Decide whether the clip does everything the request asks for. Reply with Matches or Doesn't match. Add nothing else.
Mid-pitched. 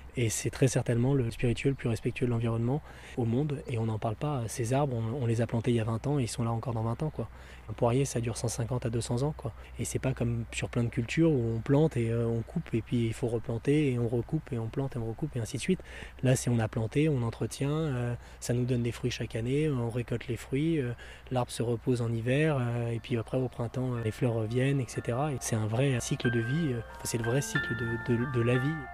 Doesn't match